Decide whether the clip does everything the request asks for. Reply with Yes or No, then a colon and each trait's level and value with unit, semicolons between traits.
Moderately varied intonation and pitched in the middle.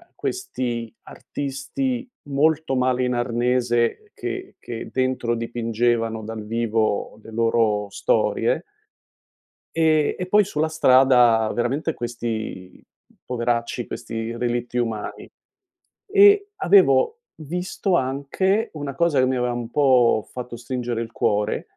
No: average, 4.3 semitones; low, 125 Hz